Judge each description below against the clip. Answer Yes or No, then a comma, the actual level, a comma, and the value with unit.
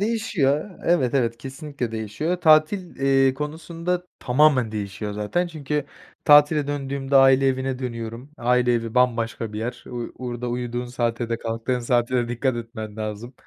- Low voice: Yes, low, 125 Hz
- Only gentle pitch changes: No, average, 3.9 semitones